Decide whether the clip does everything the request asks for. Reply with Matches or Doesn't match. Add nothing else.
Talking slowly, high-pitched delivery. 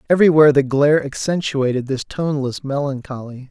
Doesn't match